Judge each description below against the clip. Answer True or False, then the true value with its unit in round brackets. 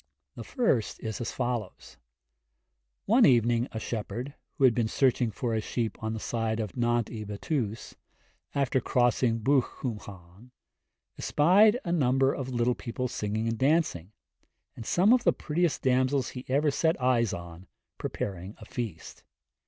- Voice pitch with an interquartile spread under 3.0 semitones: False (3.5 semitones)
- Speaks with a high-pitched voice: False (120 Hz)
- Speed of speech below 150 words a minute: False (155 wpm)